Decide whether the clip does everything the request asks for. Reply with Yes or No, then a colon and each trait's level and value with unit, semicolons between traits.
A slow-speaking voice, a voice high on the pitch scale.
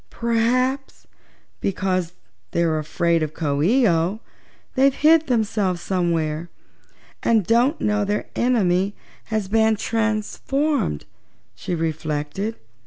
Yes: slow, 105 wpm; high, 205 Hz